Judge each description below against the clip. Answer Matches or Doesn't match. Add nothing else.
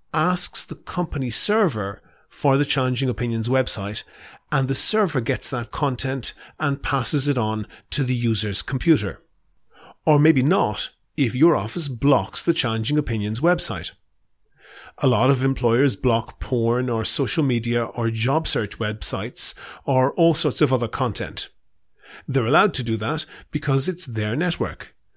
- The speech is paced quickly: Doesn't match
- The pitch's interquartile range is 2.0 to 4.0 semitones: Doesn't match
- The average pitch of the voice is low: Matches